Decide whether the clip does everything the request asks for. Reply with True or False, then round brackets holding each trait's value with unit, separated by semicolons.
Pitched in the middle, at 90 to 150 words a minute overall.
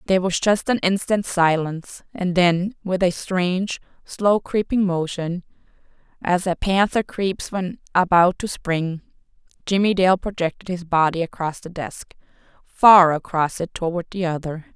True (180 Hz; 140 wpm)